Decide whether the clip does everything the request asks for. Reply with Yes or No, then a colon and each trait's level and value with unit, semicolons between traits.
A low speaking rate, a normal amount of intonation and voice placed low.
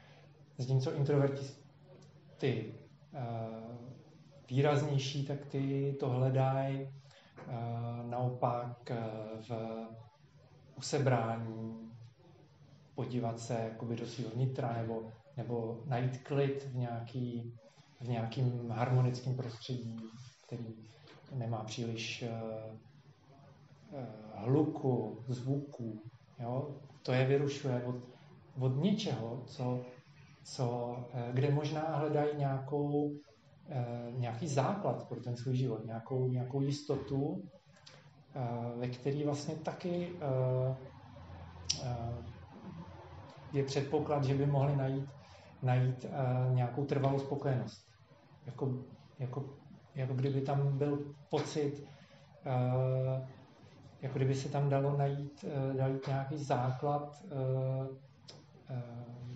Yes: slow, 85 wpm; average, 3.0 semitones; low, 130 Hz